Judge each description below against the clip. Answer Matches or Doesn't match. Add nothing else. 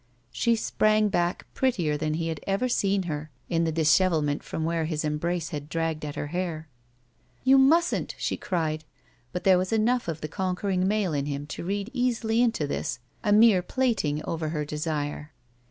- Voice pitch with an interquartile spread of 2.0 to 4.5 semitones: Doesn't match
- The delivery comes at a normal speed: Matches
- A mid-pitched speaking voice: Matches